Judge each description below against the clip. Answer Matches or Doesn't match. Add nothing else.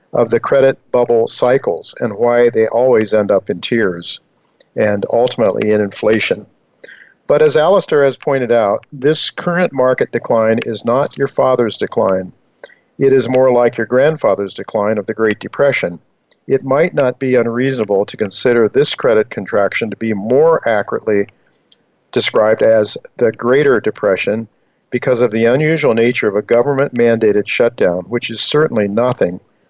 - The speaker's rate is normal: Matches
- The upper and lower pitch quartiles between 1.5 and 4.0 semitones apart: Matches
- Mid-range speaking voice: Doesn't match